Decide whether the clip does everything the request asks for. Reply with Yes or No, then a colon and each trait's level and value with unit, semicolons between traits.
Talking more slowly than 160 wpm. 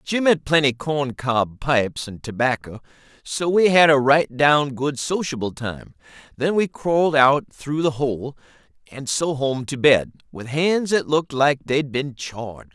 No: average, 175 wpm